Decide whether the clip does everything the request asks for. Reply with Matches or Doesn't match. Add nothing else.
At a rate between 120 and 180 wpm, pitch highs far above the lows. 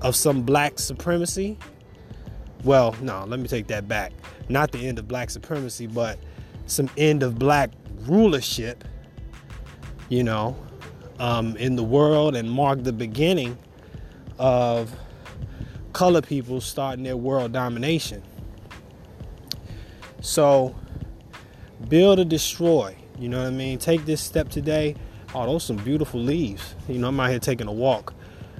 Doesn't match